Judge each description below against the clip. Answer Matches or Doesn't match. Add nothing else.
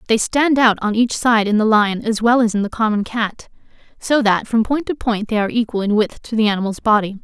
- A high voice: Matches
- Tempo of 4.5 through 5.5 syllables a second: Doesn't match